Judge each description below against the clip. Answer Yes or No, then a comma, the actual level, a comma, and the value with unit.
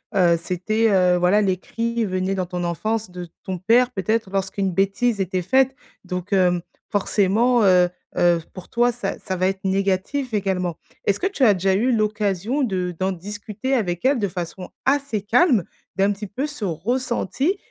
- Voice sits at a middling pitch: No, high, 195 Hz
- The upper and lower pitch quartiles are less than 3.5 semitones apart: No, average, 3.8 semitones